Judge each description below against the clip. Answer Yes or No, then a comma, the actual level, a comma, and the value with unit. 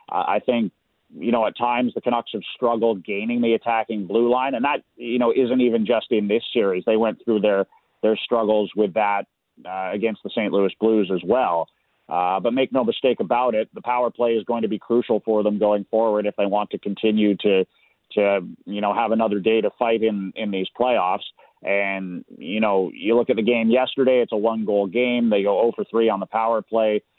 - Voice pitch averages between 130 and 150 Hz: No, low, 110 Hz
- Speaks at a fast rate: Yes, fast, 220 wpm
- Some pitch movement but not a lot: No, narrow, 2.3 semitones